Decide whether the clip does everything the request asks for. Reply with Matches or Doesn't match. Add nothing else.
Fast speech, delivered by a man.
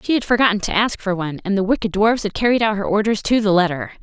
Doesn't match